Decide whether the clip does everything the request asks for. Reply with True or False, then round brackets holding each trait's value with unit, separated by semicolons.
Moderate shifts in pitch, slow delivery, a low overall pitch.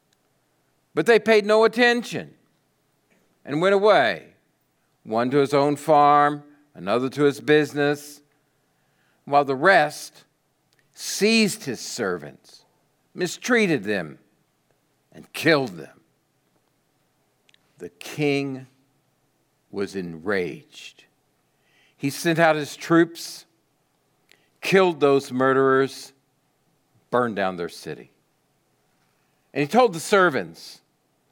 False (3.6 semitones; 95 wpm; 145 Hz)